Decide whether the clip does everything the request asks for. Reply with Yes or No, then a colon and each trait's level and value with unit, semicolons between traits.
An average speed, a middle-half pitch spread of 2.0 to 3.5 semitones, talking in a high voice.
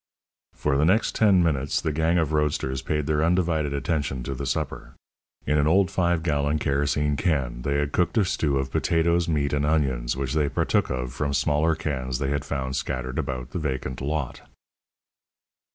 No: average, 185 wpm; average, 3.0 semitones; very low, 75 Hz